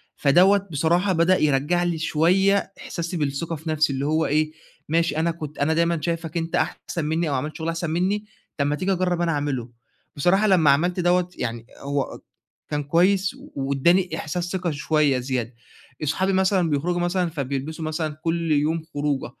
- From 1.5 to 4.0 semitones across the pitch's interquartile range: Yes, average, 3.1 semitones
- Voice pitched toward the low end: No, medium, 165 Hz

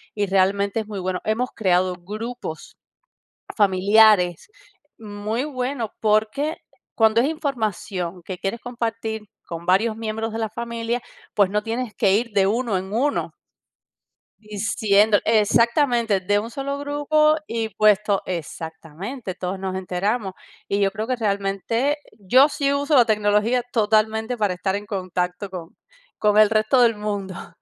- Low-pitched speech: No, high, 215 Hz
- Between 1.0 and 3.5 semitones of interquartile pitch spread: Yes, average, 3.1 semitones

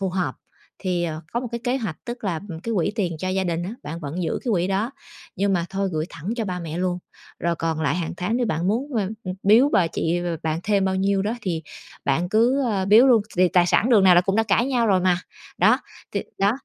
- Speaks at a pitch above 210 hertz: No, high, 190 Hz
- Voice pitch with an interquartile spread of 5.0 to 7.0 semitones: No, average, 3.9 semitones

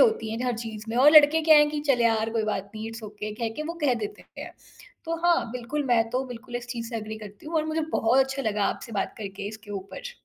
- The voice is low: No, high, 235 Hz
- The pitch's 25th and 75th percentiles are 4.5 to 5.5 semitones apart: Yes, average, 5.0 semitones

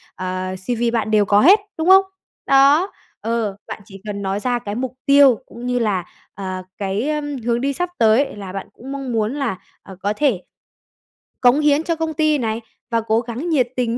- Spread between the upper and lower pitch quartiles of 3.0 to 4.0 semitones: No, average, 5.3 semitones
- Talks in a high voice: Yes, high, 235 Hz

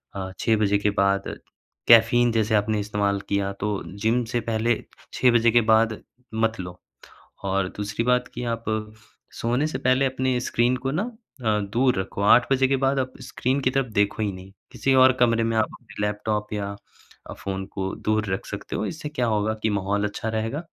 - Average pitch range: Yes, average, 3.4 semitones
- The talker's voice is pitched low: Yes, low, 110 Hz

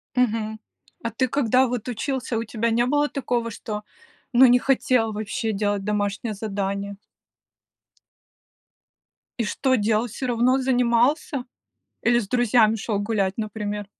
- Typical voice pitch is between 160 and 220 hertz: No, high, 230 Hz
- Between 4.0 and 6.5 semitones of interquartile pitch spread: No, average, 3.0 semitones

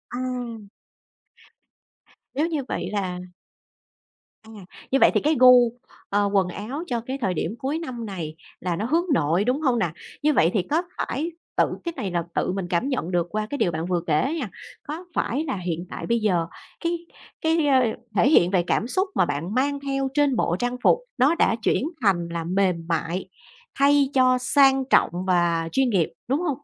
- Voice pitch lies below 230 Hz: No, high, 235 Hz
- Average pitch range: No, wide, 7.5 semitones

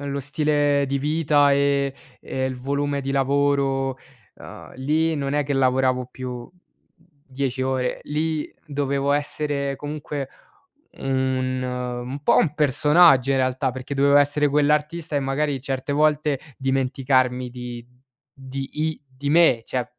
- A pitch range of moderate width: No, narrow, 1.8 semitones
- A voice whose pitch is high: No, medium, 140 Hz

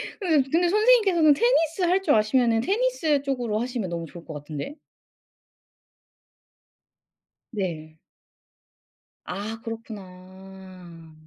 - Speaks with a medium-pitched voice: No, high, 225 Hz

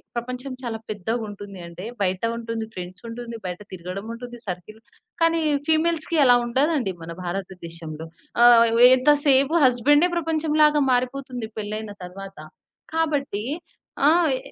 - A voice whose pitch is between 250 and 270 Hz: No, high, 235 Hz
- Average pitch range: No, wide, 6.0 semitones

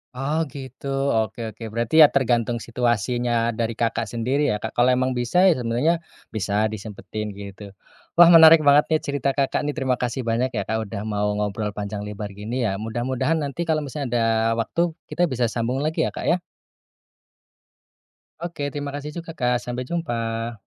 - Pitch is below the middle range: Yes, low, 120 Hz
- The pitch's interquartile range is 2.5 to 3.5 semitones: No, average, 4.1 semitones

